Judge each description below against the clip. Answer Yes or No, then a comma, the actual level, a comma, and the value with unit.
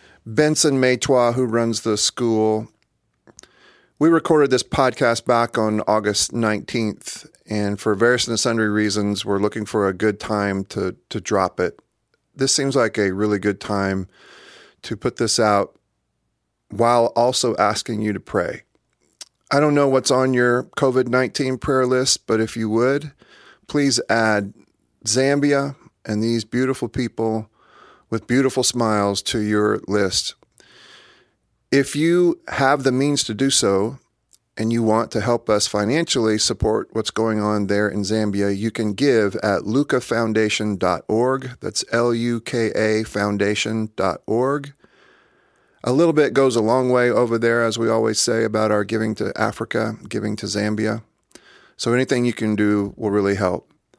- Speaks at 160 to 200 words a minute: No, average, 150 wpm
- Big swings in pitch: No, average, 3.5 semitones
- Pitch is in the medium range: No, low, 115 Hz